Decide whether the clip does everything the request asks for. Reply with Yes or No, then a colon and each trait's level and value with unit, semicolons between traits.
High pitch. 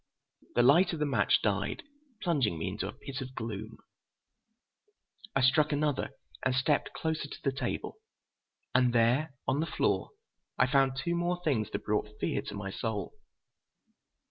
No: low, 130 Hz